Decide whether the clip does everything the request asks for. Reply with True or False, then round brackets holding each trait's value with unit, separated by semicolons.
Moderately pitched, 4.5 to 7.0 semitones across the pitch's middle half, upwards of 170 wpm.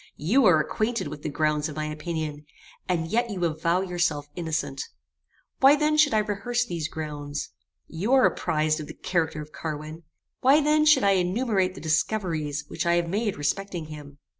True (170 Hz; 5.5 semitones; 180 wpm)